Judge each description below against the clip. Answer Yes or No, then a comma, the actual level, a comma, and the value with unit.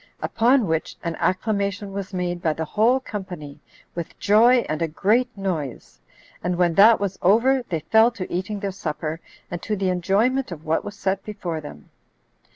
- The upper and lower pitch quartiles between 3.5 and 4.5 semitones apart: Yes, average, 4.2 semitones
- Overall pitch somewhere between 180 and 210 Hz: Yes, high, 190 Hz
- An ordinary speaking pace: Yes, average, 175 wpm